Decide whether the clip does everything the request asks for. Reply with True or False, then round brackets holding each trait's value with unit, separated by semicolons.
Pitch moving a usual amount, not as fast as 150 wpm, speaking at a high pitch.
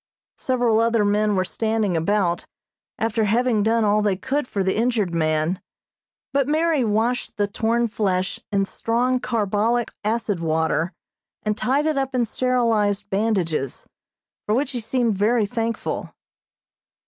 True (3.2 semitones; 140 wpm; 220 Hz)